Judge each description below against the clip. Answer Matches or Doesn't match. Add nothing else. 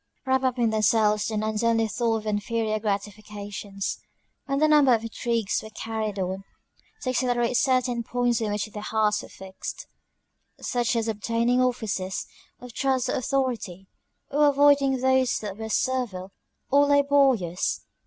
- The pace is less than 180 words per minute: Matches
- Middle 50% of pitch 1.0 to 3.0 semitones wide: Doesn't match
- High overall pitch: Matches